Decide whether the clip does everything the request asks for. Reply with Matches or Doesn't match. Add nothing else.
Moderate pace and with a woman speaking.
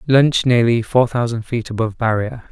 Doesn't match